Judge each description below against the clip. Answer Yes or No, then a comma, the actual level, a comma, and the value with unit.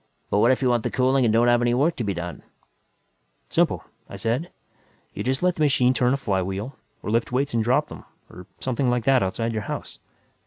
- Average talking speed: No, fast, 225 wpm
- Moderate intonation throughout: Yes, average, 3.0 semitones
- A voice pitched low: Yes, low, 120 Hz